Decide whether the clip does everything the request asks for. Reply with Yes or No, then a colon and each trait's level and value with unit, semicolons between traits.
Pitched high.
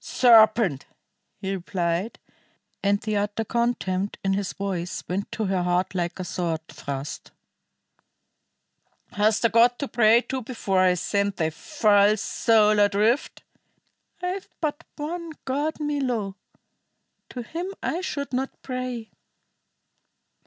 Yes: high, 215 Hz